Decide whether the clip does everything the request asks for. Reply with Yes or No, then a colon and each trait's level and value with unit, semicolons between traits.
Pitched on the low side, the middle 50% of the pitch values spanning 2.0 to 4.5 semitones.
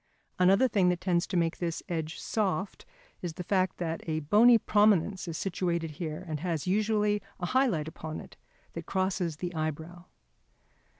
No: medium, 180 Hz; average, 3.2 semitones